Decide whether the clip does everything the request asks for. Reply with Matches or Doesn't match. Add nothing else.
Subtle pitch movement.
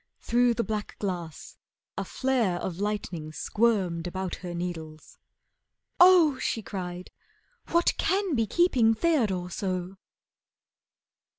Doesn't match